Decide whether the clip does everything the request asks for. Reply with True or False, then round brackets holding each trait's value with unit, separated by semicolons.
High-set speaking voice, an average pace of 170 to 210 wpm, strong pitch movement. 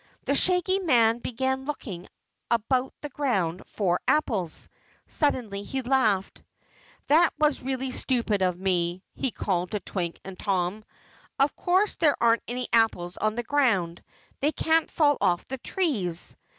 False (235 Hz; 145 wpm; 6.7 semitones)